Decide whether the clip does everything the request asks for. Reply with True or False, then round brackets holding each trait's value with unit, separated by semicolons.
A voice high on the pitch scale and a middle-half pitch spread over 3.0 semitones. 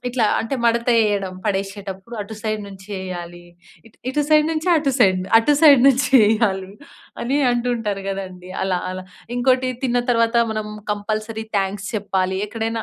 True (215 Hz; 3.9 semitones)